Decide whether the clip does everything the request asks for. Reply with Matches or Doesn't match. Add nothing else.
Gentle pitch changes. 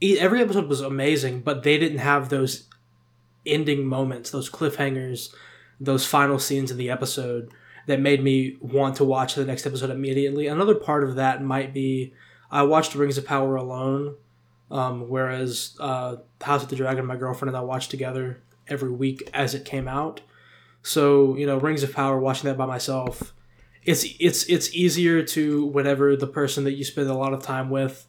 Matches